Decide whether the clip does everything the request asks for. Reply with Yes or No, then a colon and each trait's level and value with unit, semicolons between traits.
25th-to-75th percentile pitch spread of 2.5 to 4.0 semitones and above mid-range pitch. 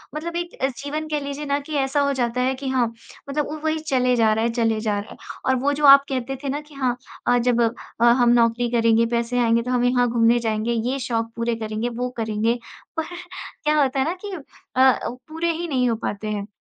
Yes: average, 3.4 semitones; very high, 250 Hz